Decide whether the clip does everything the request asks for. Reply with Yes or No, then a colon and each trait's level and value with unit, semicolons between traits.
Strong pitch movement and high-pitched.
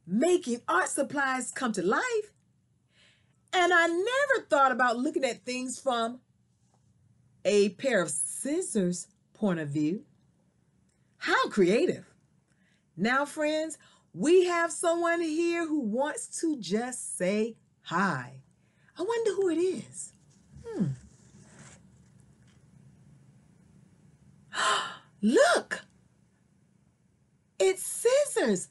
Yes: wide, 9.0 semitones; very high, 265 Hz